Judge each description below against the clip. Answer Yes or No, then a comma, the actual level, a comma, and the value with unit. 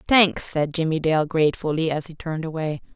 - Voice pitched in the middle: Yes, medium, 160 Hz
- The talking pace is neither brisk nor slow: Yes, average, 185 wpm